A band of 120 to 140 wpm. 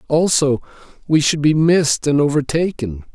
Yes: slow, 135 wpm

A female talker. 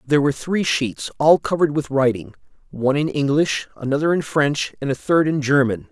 No: male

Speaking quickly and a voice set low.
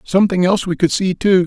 No: fast, 245 wpm; medium, 185 Hz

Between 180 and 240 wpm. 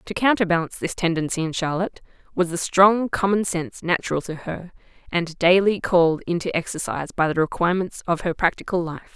No: average, 170 wpm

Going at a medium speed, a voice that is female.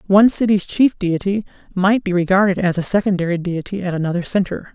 Yes: average, 175 wpm; female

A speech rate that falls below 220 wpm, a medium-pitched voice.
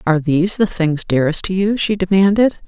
Yes: average, 200 wpm; medium, 180 Hz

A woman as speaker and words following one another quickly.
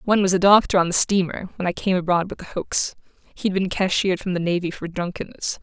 Yes: female; fast, 235 wpm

